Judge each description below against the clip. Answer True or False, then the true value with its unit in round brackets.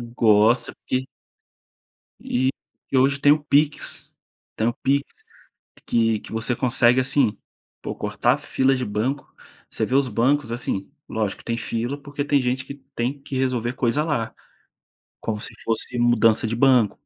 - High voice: False (125 Hz)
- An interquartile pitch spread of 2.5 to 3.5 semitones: True (3.2 semitones)